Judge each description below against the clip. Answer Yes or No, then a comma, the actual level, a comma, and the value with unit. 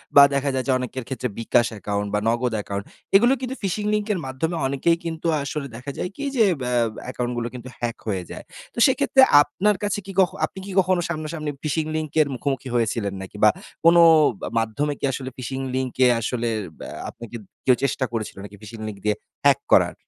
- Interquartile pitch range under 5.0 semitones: No, wide, 5.6 semitones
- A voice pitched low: Yes, low, 130 Hz